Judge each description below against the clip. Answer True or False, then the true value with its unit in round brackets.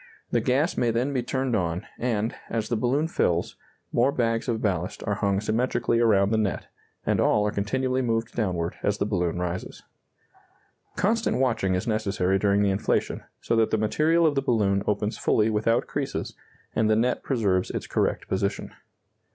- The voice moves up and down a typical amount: True (3.7 semitones)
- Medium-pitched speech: False (110 Hz)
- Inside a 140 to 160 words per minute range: False (175 wpm)